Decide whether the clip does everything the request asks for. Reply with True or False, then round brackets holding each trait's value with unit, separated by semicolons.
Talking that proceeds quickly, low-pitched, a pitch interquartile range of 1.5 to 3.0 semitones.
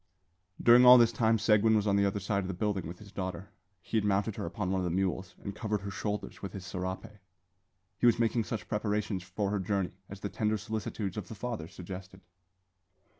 True (220 wpm; 100 Hz; 2.5 semitones)